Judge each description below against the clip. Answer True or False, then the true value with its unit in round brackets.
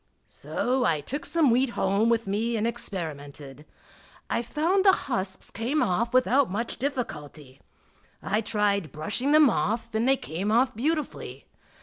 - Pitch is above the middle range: True (230 Hz)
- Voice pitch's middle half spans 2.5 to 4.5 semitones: False (5.5 semitones)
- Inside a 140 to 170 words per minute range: True (145 wpm)